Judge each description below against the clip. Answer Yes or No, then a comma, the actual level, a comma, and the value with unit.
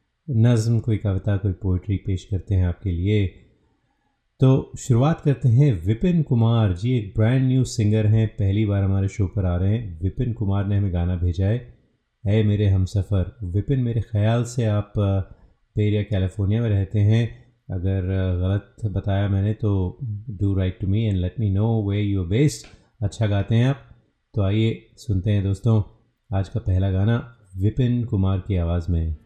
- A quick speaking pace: No, average, 175 wpm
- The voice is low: Yes, low, 105 Hz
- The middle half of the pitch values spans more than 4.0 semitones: No, average, 3.0 semitones